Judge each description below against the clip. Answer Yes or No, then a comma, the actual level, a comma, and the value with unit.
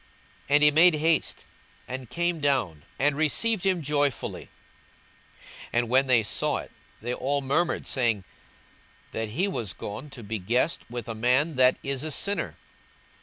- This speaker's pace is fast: No, average, 165 wpm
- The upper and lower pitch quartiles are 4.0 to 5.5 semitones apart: Yes, average, 4.6 semitones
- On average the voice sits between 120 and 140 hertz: Yes, low, 135 Hz